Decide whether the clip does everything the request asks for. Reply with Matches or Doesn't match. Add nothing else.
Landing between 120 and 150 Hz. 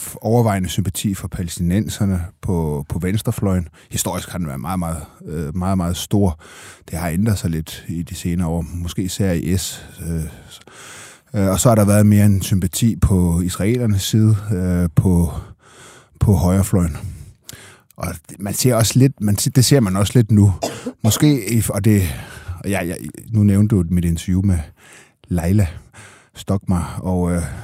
Doesn't match